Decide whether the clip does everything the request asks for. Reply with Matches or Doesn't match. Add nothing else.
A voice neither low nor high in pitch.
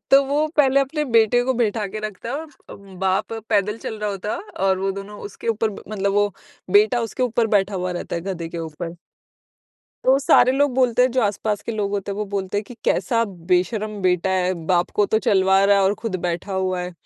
Doesn't match